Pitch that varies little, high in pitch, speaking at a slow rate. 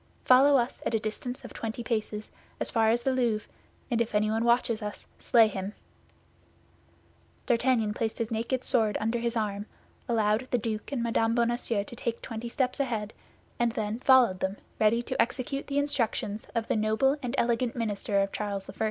No: narrow, 2.1 semitones; high, 230 Hz; average, 180 wpm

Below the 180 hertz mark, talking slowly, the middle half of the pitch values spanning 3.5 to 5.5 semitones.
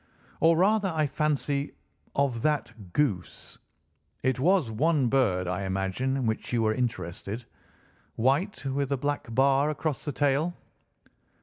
Yes: low, 135 Hz; slow, 130 wpm; average, 4.7 semitones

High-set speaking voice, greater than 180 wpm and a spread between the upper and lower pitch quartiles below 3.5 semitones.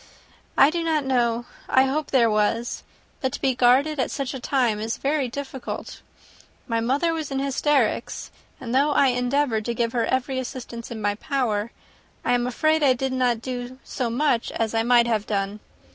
Yes: very high, 250 Hz; average, 190 wpm; average, 2.9 semitones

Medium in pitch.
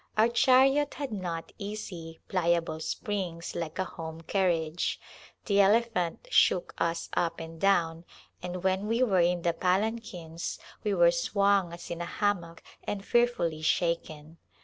Yes: medium, 180 Hz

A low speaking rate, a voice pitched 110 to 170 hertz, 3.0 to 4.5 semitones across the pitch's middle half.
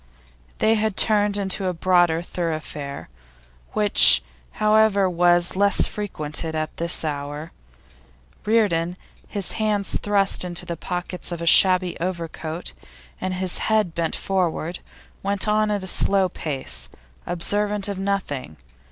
No: slow, 125 wpm; medium, 185 Hz; average, 3.4 semitones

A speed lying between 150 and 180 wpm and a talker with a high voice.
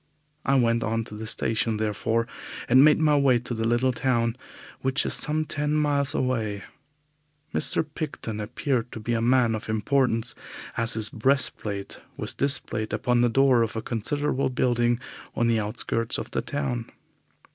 No: average, 170 wpm; low, 120 Hz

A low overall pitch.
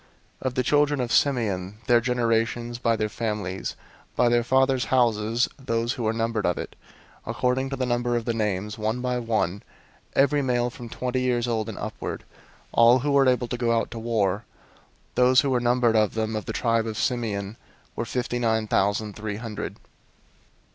Yes: low, 120 Hz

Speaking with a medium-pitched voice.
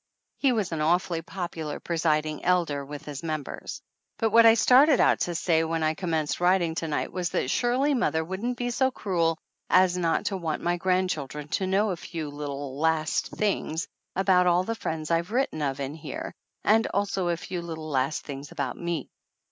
Yes: medium, 170 Hz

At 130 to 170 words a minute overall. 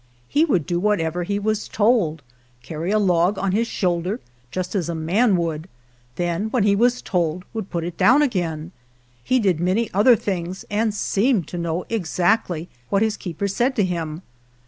No: average, 185 wpm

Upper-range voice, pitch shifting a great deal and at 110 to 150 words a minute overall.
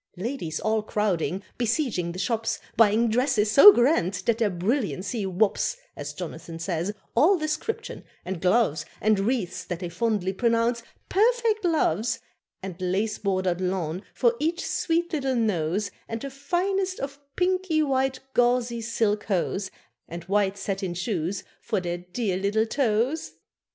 Yes: high, 220 Hz; wide, 6.0 semitones; average, 140 wpm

